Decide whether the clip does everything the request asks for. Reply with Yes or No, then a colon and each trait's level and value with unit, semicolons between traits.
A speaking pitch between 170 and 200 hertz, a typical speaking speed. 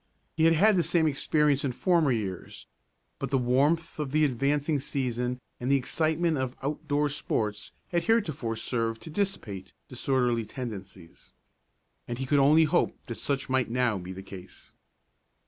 No: low, 135 Hz; average, 165 wpm